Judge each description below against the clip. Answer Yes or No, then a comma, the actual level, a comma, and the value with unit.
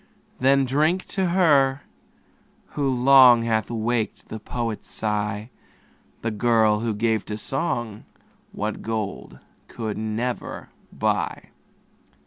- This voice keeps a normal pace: No, slow, 110 wpm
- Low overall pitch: Yes, low, 115 Hz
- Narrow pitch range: No, average, 3.7 semitones